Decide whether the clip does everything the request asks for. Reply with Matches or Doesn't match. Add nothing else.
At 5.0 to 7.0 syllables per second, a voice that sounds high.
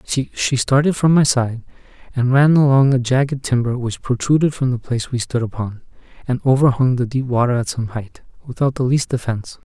Doesn't match